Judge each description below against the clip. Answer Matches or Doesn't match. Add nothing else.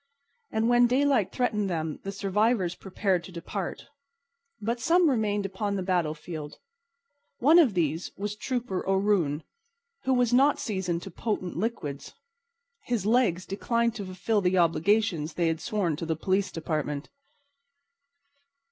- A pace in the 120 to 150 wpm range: Matches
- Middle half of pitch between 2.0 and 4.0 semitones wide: Doesn't match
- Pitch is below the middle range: Doesn't match